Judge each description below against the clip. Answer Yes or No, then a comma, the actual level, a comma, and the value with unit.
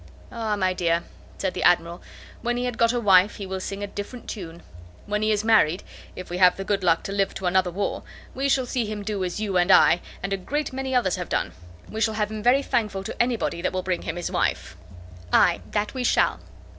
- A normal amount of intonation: Yes, average, 3.6 semitones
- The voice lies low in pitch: No, high, 200 Hz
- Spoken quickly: Yes, fast, 240 wpm